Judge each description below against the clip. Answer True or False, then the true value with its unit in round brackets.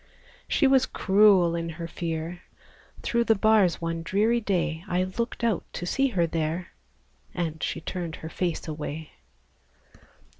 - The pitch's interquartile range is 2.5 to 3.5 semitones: False (4.2 semitones)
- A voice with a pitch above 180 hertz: False (175 Hz)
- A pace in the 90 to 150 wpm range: True (145 wpm)